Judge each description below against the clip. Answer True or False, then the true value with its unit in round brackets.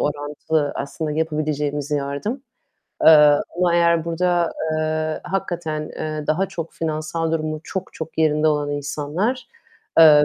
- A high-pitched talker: False (155 Hz)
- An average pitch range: False (2.2 semitones)